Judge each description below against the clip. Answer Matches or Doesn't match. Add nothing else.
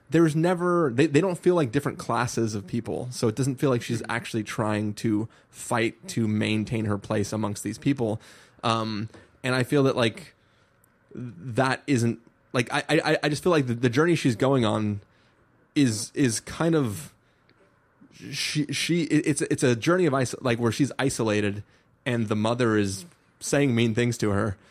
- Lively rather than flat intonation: Doesn't match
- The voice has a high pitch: Doesn't match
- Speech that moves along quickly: Doesn't match